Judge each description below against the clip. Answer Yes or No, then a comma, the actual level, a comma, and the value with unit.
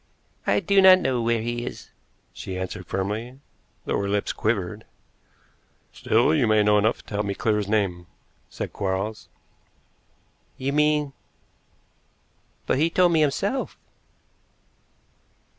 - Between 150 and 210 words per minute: No, slow, 135 wpm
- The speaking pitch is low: Yes, low, 110 Hz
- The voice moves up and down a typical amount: No, wide, 6.3 semitones